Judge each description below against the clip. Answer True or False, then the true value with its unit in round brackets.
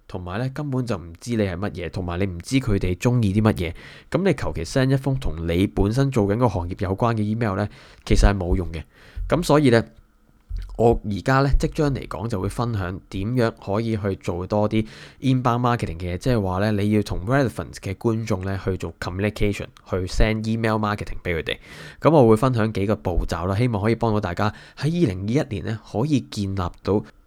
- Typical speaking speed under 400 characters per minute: False (405 characters per minute)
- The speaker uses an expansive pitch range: False (4.0 semitones)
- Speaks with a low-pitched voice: True (105 Hz)